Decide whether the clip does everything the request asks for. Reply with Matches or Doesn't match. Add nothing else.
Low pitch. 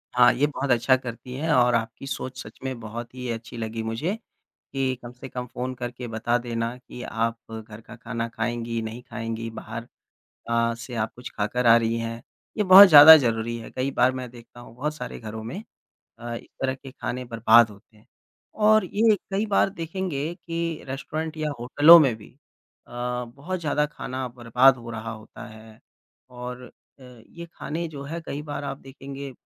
Matches